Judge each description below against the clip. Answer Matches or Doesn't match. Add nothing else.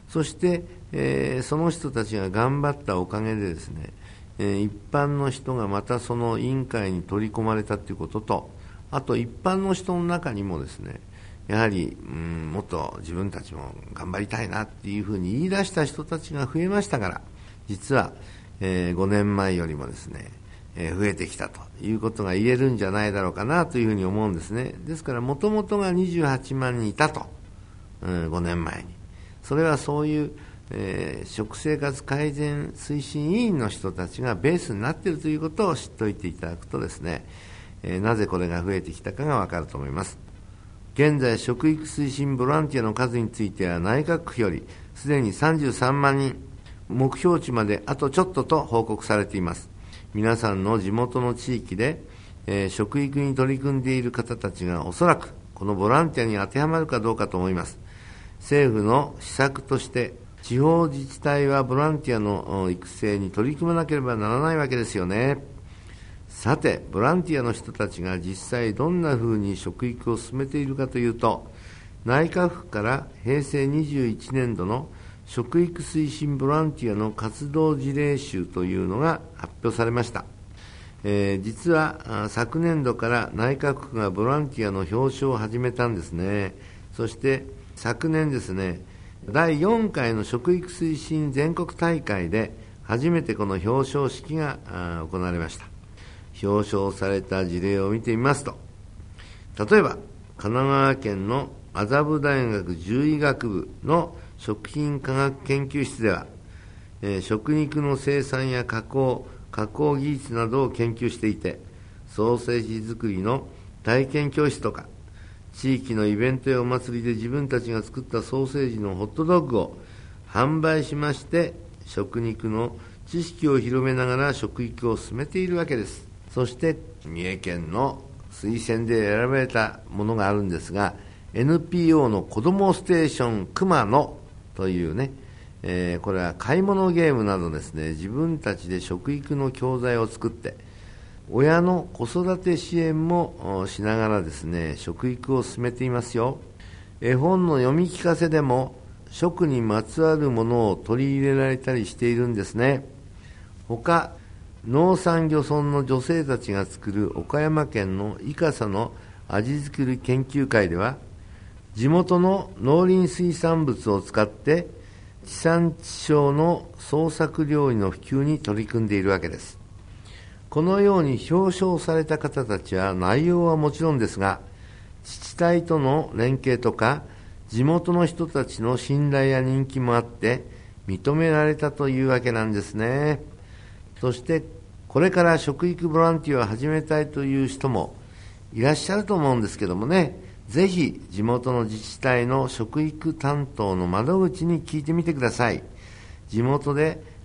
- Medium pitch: Doesn't match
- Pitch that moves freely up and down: Matches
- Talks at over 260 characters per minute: Matches